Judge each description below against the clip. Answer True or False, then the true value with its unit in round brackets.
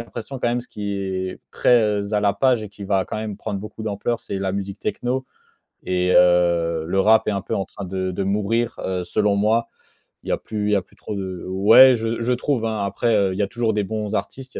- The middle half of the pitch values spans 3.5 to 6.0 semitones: False (2.7 semitones)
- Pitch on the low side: True (105 Hz)